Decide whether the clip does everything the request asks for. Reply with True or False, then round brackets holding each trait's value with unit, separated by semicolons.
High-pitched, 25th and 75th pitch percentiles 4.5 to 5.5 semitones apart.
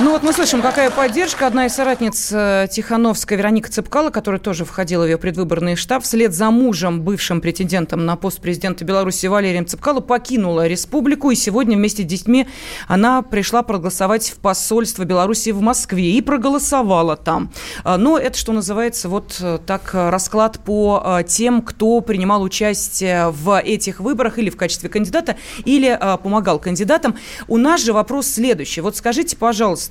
True (210 Hz; 4.8 semitones)